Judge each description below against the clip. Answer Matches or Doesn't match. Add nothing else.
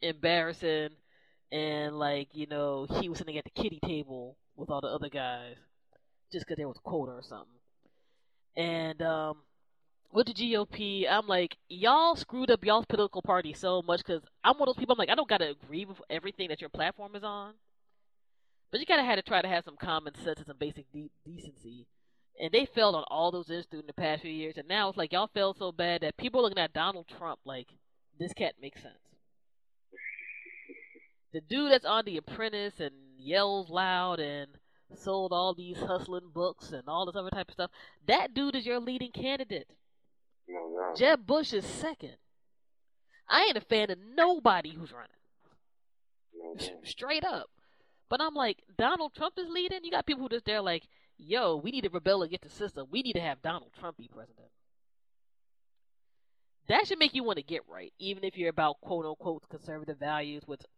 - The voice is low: Doesn't match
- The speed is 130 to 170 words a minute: Doesn't match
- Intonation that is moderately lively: Doesn't match